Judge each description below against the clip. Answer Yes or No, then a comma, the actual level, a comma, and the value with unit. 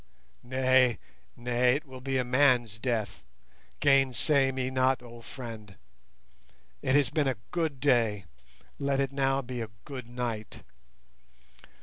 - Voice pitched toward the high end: No, low, 130 Hz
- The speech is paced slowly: Yes, slow, 125 wpm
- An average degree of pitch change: No, narrow, 2.1 semitones